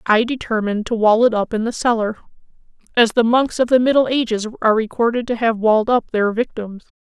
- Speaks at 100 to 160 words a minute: No, average, 195 wpm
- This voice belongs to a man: No, female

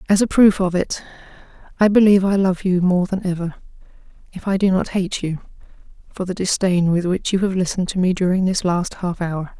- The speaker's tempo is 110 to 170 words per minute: No, average, 200 wpm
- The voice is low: No, medium, 185 Hz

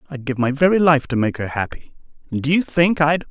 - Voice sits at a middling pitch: Yes, medium, 145 Hz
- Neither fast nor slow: No, fast, 255 wpm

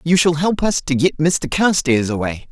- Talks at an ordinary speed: No, fast, 215 wpm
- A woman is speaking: No, male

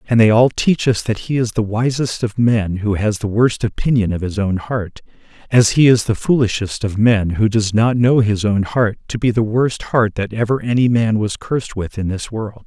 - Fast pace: Yes, fast, 235 wpm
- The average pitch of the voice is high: No, low, 110 Hz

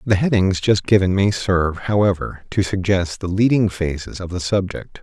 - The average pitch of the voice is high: No, very low, 95 Hz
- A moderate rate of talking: Yes, average, 180 wpm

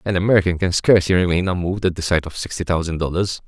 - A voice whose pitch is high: No, very low, 90 Hz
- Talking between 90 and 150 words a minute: No, fast, 225 wpm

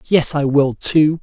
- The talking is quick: No, average, 195 wpm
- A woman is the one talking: No, male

